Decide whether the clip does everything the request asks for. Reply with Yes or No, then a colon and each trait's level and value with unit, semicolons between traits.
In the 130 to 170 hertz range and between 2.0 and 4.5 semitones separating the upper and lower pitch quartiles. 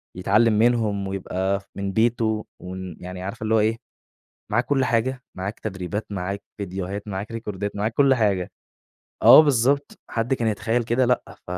No: low, 105 Hz; average, 3.4 semitones